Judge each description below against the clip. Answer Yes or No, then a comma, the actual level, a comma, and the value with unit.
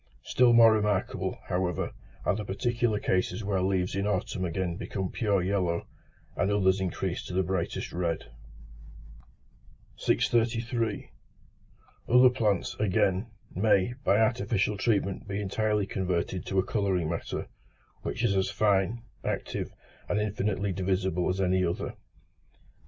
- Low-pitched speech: Yes, low, 100 Hz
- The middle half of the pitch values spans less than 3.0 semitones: Yes, narrow, 2.4 semitones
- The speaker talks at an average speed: No, slow, 130 wpm